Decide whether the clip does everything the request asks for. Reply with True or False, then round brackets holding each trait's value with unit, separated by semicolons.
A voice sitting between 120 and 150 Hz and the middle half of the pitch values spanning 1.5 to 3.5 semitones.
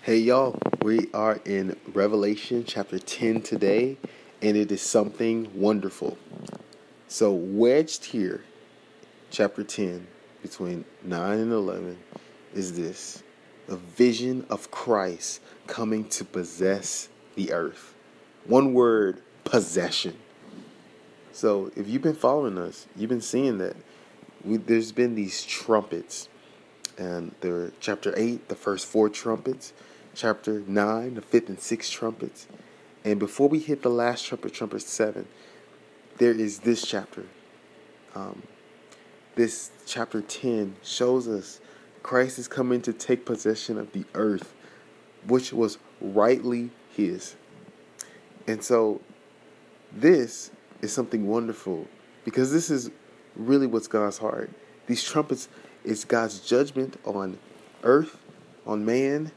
False (110 Hz; 3.0 semitones)